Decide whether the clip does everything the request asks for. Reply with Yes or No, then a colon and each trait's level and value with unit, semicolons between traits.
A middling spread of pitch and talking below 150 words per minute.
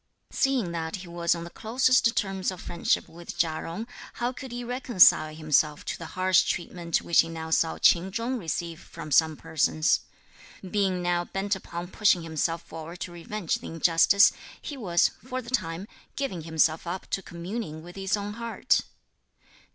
No: average, 4.0 semitones; average, 175 wpm